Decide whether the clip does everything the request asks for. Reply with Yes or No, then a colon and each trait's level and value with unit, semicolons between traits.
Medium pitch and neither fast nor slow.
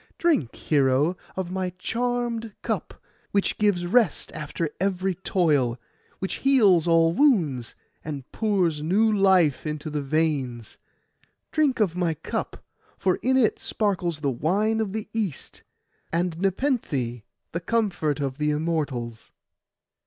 No: medium, 175 Hz; slow, 130 wpm